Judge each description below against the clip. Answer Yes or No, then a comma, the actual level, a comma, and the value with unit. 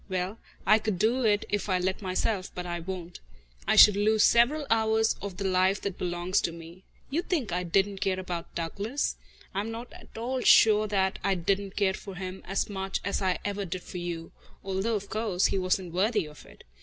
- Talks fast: Yes, fast, 210 wpm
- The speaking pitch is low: No, high, 195 Hz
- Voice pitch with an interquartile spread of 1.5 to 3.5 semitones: Yes, average, 2.7 semitones